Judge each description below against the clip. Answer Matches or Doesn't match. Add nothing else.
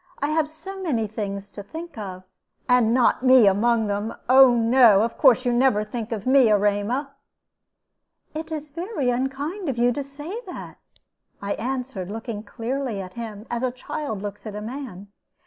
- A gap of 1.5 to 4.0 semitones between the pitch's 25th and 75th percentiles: Doesn't match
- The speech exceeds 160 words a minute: Matches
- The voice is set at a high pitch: Matches